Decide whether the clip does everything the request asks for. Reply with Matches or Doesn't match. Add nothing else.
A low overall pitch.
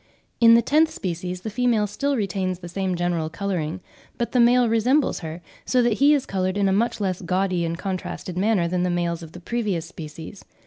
Doesn't match